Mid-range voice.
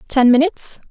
No: very high, 280 Hz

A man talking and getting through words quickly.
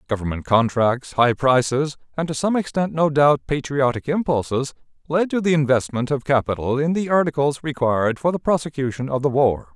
No: male; average, 170 wpm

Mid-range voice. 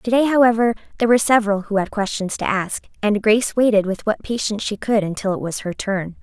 No: high, 210 Hz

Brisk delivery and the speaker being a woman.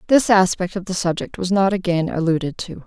Yes: fast, 210 wpm; female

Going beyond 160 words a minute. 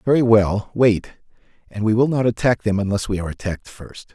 Yes: fast, 205 wpm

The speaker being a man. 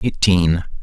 Yes: male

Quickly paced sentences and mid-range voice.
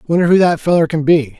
Yes: fast, 260 wpm; medium, 160 Hz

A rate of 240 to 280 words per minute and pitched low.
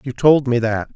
Yes: fast, 250 wpm; low, 125 Hz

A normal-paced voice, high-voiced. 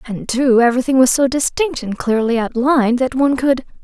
Yes: average, 190 wpm; very high, 255 Hz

